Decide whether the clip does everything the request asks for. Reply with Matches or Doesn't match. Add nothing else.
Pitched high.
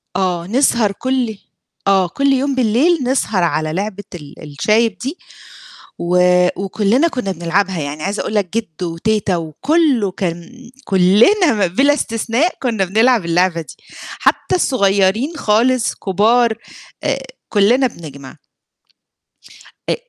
Matches